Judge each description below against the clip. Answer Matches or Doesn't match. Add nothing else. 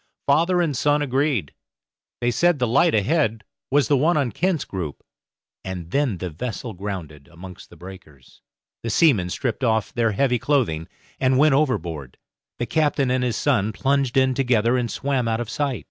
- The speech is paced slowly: Doesn't match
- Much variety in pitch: Matches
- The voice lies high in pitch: Doesn't match